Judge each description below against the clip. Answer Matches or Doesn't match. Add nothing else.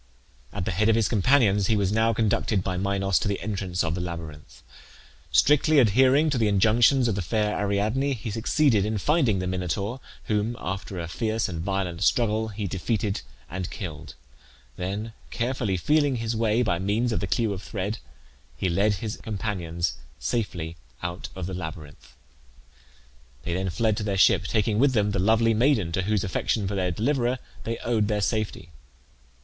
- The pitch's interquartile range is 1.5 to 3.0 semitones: Doesn't match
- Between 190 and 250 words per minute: Doesn't match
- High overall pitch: Doesn't match